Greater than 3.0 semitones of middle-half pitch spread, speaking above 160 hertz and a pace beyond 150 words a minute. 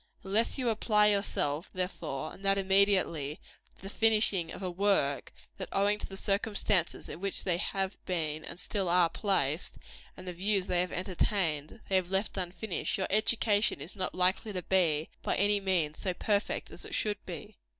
No: average, 2.7 semitones; high, 190 Hz; average, 180 wpm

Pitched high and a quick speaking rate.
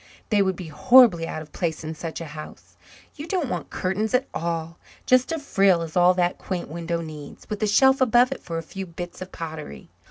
No: medium, 175 Hz; fast, 220 wpm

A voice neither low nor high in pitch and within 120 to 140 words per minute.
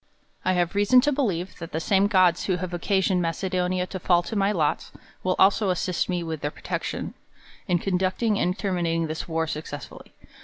No: medium, 180 Hz; average, 195 wpm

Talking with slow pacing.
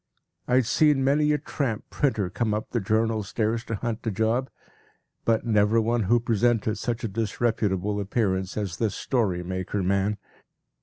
No: average, 165 wpm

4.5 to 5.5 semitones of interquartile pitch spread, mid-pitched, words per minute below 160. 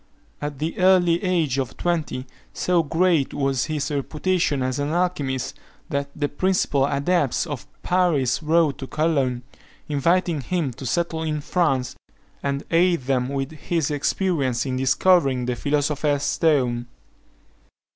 No: average, 4.0 semitones; medium, 145 Hz; slow, 135 wpm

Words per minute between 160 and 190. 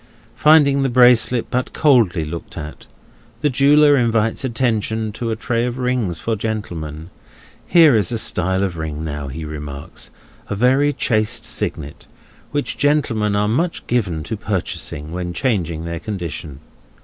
No: average, 140 wpm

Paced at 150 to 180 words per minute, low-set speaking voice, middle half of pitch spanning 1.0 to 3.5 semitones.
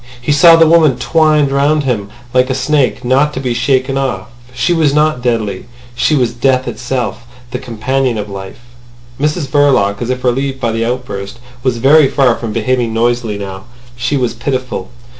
Yes: average, 175 wpm; low, 125 Hz; average, 2.9 semitones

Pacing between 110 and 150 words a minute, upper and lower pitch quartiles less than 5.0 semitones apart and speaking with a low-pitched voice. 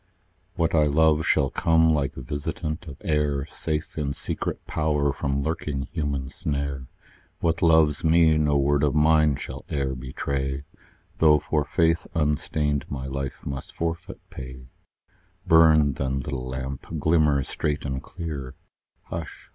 Yes: average, 140 wpm; narrow, 2.5 semitones; very low, 75 Hz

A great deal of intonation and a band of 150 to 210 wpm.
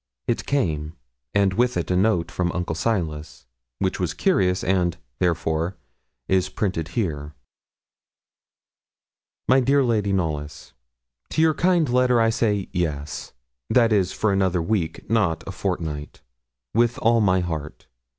No: wide, 5.7 semitones; slow, 135 wpm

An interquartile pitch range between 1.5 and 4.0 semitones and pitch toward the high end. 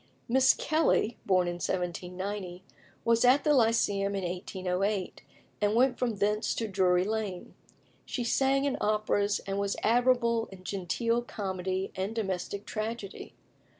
Yes: average, 3.6 semitones; high, 205 Hz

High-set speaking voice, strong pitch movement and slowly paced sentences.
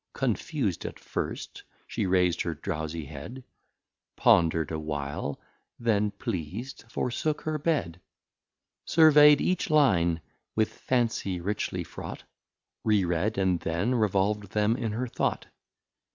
No: low, 105 Hz; wide, 6.3 semitones; slow, 120 wpm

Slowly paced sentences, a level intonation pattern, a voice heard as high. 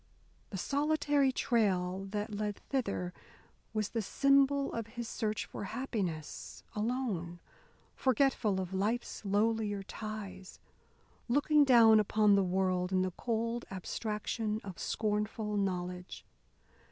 No: slow, 115 wpm; average, 3.6 semitones; high, 210 Hz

